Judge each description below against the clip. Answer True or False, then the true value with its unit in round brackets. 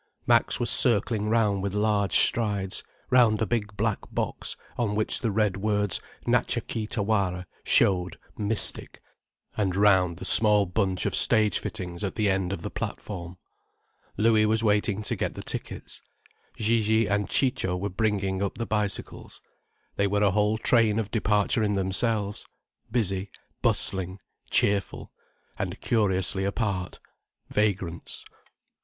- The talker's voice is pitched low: True (105 Hz)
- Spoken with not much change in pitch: True (2.1 semitones)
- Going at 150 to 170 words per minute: False (135 wpm)